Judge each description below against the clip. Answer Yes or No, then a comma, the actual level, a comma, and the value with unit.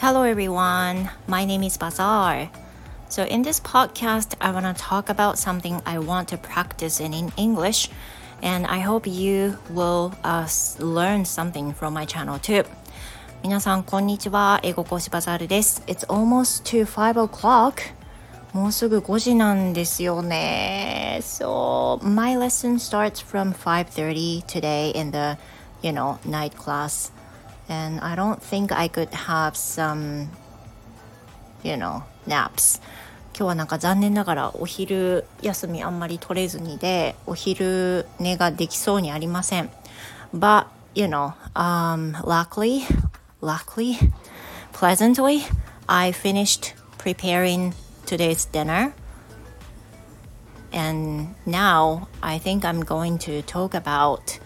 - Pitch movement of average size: Yes, average, 3.9 semitones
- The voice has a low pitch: No, medium, 180 Hz